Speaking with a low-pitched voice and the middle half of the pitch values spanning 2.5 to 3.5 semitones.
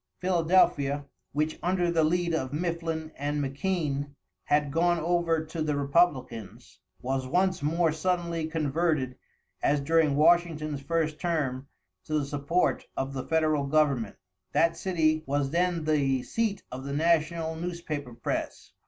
No: medium, 155 Hz; average, 3.1 semitones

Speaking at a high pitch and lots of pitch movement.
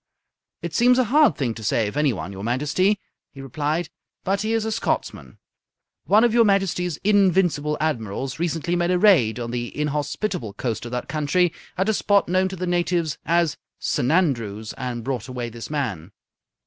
No: medium, 155 Hz; wide, 7.3 semitones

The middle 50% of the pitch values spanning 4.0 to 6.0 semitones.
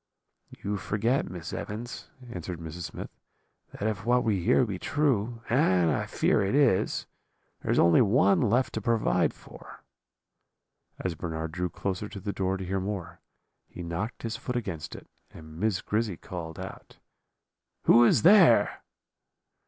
Yes: average, 4.7 semitones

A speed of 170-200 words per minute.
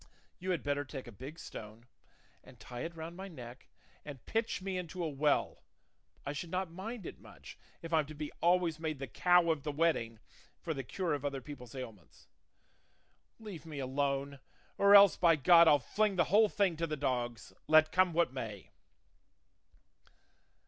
Yes: average, 180 wpm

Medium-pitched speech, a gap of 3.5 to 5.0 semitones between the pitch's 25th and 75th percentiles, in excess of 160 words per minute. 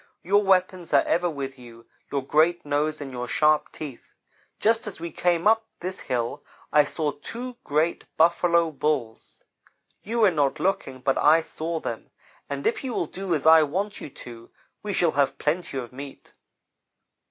Yes: medium, 160 Hz; average, 4.6 semitones; average, 175 wpm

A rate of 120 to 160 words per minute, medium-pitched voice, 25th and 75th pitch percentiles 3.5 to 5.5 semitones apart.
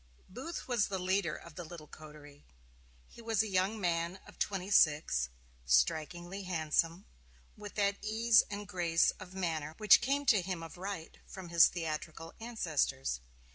Yes: average, 155 wpm; medium, 180 Hz; average, 4.2 semitones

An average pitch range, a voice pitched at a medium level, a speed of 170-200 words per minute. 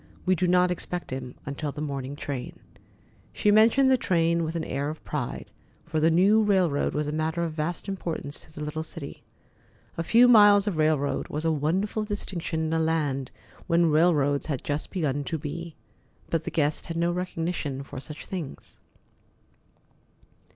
Yes: average, 3.3 semitones; medium, 160 Hz; average, 175 wpm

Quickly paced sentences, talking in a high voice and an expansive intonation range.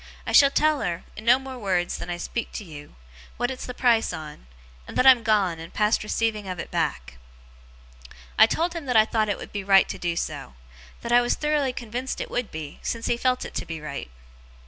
Yes: fast, 230 wpm; high, 220 Hz; wide, 6.2 semitones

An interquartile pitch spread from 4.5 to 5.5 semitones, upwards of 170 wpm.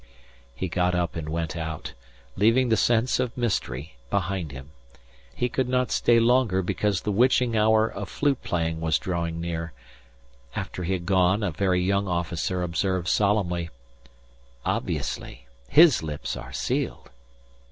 No: average, 4.8 semitones; average, 145 wpm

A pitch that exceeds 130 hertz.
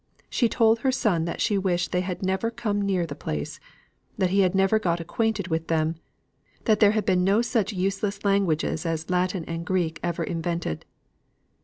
Yes: medium, 185 Hz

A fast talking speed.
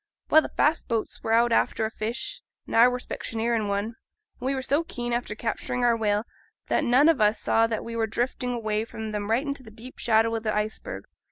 Yes: fast, 235 wpm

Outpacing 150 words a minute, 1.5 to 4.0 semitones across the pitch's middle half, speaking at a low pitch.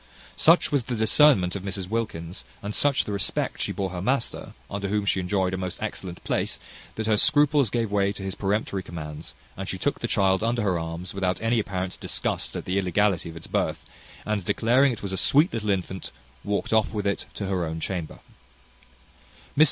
Yes: average, 200 wpm; average, 3.2 semitones; low, 100 Hz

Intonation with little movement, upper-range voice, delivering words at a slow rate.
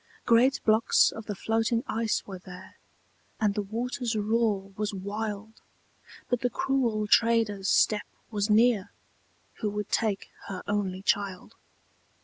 Yes: narrow, 2.2 semitones; high, 215 Hz; slow, 130 wpm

